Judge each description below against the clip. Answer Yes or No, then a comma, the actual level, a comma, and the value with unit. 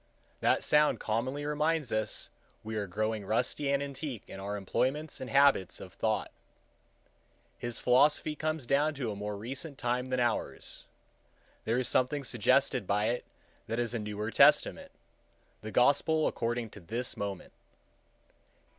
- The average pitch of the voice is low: Yes, low, 125 Hz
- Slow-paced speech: No, average, 145 wpm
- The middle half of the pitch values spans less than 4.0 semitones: No, average, 4.6 semitones